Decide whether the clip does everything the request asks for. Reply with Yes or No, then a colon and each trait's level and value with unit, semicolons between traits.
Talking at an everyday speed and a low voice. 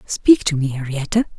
No: average, 175 wpm; medium, 170 Hz